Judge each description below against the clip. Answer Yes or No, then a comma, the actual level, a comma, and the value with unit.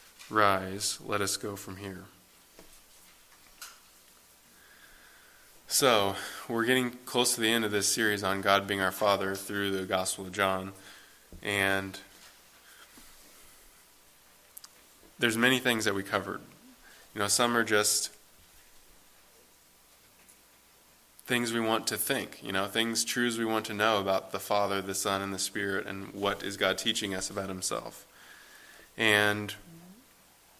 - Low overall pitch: Yes, low, 100 Hz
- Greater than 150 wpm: No, slow, 135 wpm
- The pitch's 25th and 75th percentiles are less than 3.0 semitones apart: Yes, narrow, 2.6 semitones